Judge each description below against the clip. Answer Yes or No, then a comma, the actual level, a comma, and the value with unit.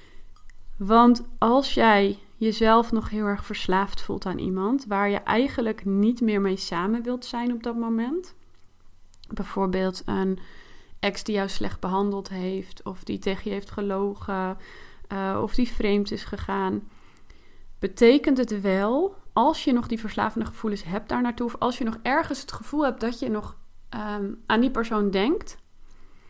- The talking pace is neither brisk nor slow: Yes, average, 160 wpm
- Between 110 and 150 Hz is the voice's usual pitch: No, high, 215 Hz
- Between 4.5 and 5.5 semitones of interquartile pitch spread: No, average, 3.5 semitones